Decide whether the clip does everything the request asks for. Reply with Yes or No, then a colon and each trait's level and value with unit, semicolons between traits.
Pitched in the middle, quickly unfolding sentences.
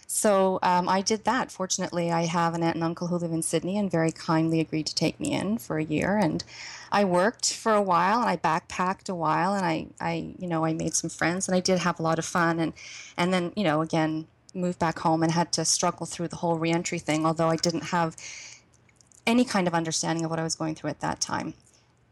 Yes: medium, 170 Hz; fast, 245 wpm